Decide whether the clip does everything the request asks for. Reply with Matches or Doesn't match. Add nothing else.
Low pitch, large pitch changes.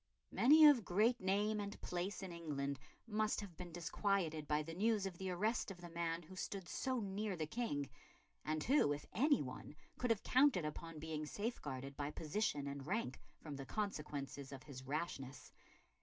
Doesn't match